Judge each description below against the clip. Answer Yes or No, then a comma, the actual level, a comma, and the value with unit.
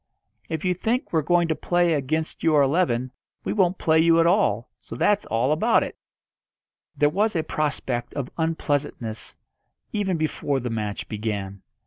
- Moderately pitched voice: Yes, medium, 155 Hz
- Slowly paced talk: No, average, 160 wpm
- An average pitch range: No, wide, 5.8 semitones